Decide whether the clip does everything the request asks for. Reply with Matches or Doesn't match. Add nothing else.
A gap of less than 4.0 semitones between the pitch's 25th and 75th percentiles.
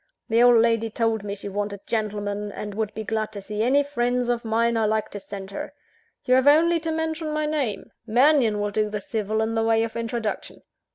Matches